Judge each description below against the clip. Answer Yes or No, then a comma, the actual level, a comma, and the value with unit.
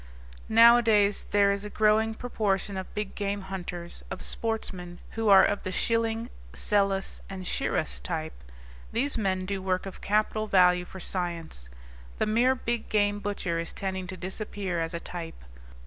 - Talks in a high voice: Yes, high, 200 Hz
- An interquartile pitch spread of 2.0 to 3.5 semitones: Yes, average, 2.8 semitones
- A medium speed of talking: Yes, average, 160 wpm